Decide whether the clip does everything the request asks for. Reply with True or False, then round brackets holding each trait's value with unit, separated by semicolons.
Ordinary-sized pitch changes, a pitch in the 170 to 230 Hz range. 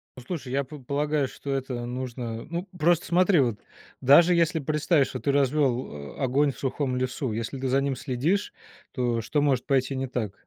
False (3.1 semitones; 135 Hz)